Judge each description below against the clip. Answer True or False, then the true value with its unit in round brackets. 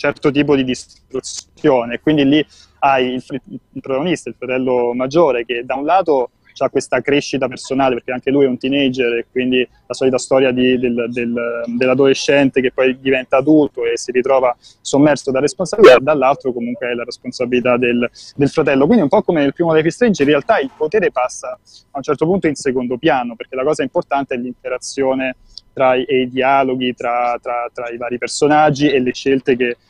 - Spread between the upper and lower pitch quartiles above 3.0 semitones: False (2.5 semitones)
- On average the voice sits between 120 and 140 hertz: True (130 Hz)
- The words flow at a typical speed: False (195 wpm)